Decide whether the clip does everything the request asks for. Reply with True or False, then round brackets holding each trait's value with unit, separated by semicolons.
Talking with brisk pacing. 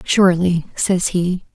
False (115 wpm)